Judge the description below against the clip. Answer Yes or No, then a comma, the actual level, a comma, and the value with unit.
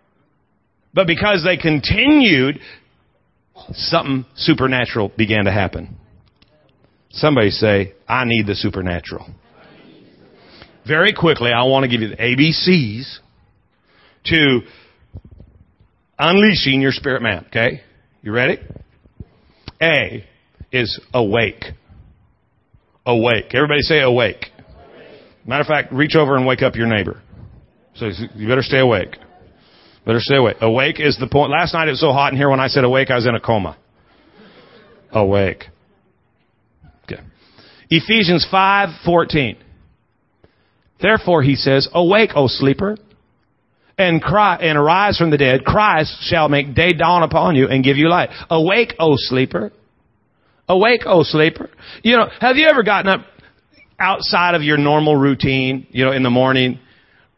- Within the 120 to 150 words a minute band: Yes, slow, 135 wpm